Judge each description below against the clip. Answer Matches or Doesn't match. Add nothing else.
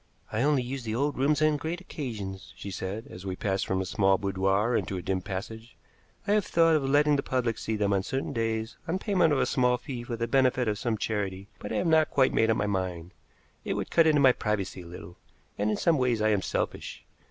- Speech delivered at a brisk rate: Matches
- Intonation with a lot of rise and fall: Matches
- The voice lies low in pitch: Matches